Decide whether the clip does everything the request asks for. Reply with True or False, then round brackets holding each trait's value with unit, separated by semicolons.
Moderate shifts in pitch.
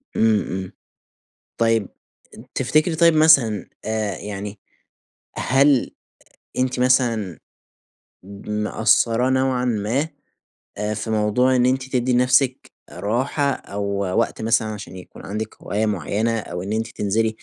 True (3.5 semitones)